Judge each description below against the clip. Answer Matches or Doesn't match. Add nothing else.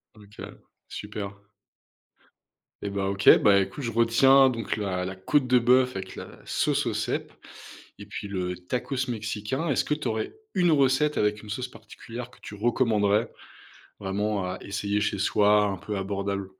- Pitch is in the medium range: Doesn't match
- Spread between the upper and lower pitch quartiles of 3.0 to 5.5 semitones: Matches